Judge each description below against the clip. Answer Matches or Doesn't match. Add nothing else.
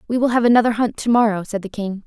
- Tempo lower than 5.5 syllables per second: Doesn't match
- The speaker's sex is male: Doesn't match